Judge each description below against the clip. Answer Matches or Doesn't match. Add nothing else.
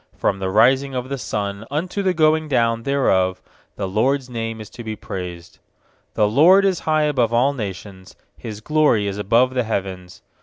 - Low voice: Matches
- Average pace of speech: Matches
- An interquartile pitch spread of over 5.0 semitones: Matches